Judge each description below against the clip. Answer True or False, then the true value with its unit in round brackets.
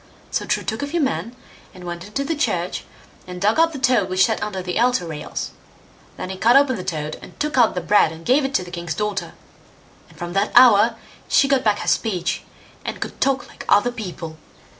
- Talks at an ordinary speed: False (225 wpm)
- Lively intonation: True (6.3 semitones)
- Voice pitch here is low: False (210 Hz)